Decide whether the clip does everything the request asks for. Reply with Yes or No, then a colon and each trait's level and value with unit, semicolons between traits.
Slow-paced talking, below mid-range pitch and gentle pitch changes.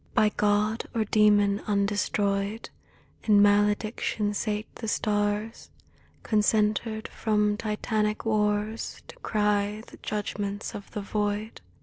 No: slow, 105 wpm; high, 210 Hz; narrow, 0.8 semitones